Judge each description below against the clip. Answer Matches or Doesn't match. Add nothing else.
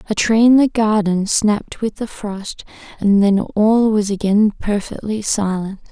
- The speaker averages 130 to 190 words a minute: Matches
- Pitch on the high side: Matches